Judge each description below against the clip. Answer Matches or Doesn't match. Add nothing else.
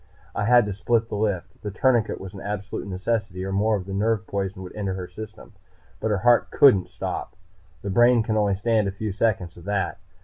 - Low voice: Matches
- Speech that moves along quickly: Matches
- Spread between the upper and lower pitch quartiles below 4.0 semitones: Matches